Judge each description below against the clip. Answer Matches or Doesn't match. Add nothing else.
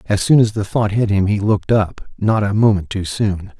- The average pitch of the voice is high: Doesn't match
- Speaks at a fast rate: Matches